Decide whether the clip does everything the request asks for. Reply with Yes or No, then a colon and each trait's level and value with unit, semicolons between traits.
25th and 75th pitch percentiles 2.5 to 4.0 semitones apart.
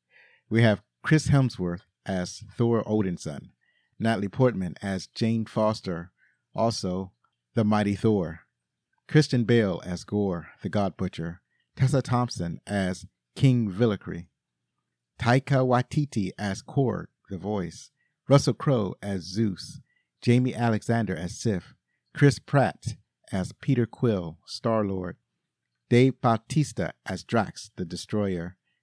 No: average, 4.7 semitones